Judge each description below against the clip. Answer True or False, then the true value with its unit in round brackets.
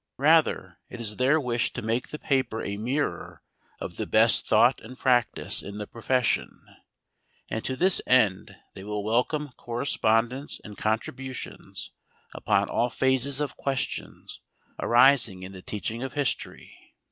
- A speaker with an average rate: True (145 wpm)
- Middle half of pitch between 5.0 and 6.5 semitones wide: False (3.5 semitones)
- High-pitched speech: False (125 Hz)